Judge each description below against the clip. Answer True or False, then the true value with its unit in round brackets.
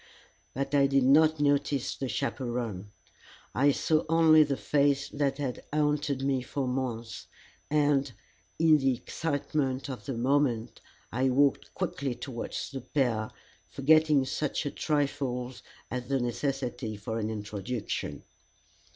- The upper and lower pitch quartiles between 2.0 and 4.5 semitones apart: True (2.6 semitones)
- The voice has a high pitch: False (135 Hz)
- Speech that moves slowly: True (130 wpm)